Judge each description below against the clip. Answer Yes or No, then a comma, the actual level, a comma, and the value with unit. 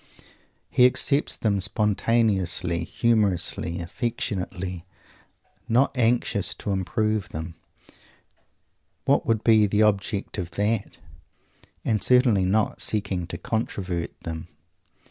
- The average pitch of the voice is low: Yes, low, 105 Hz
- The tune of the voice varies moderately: Yes, average, 3.8 semitones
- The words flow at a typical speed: No, slow, 100 wpm